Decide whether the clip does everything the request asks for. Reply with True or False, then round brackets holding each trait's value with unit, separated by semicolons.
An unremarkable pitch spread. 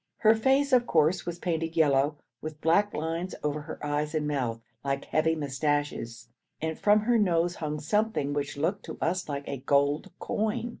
True (4.3 semitones)